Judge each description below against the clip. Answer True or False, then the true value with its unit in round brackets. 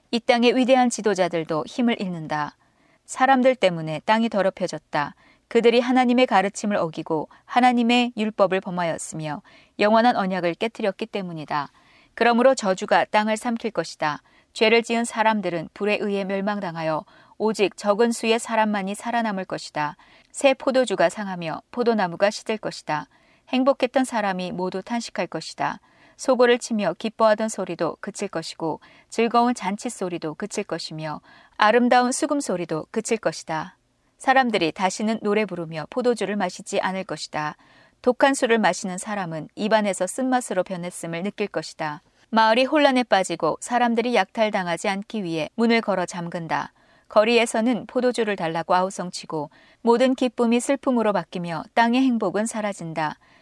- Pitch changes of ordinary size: True (5.0 semitones)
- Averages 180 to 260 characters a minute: False (350 characters per minute)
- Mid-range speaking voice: False (210 Hz)